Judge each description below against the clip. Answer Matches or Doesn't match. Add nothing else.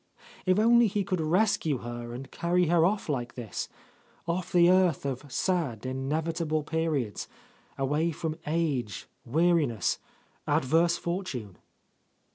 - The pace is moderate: Doesn't match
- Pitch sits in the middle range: Matches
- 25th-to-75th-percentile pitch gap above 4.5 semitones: Matches